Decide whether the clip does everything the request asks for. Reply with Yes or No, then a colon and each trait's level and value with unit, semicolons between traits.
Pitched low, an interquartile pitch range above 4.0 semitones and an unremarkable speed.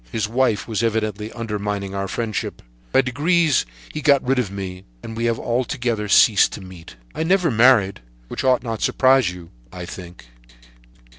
Yes: low, 115 Hz; average, 4.4 semitones; average, 170 wpm